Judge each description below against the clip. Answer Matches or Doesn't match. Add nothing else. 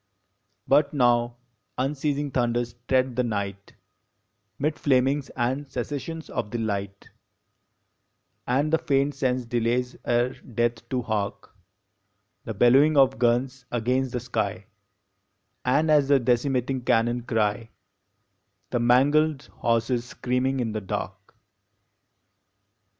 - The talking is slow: Matches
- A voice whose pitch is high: Doesn't match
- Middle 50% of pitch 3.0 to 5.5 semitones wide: Doesn't match